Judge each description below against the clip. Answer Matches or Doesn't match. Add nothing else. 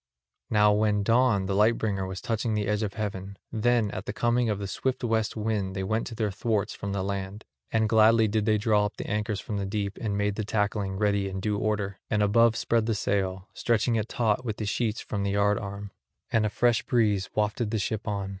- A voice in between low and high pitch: Doesn't match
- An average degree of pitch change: Doesn't match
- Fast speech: Matches